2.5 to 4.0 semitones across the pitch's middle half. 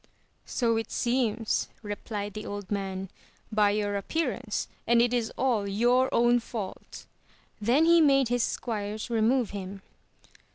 Yes: average, 3.1 semitones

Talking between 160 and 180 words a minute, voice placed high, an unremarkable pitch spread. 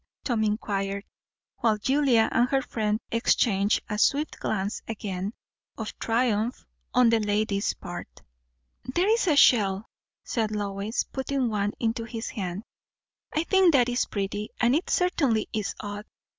No: average, 145 wpm; high, 220 Hz; average, 3.5 semitones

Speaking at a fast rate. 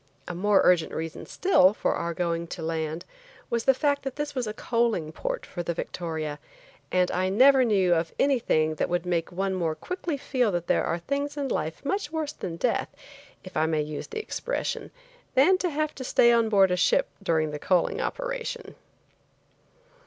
No: average, 190 wpm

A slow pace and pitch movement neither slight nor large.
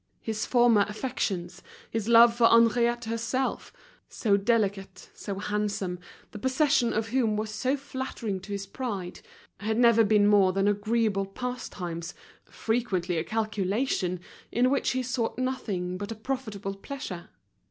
Yes: slow, 130 wpm; average, 3.4 semitones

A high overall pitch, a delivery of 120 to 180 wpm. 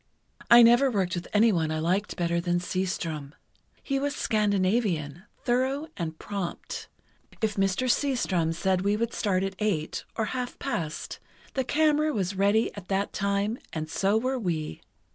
Yes: high, 200 Hz; average, 150 wpm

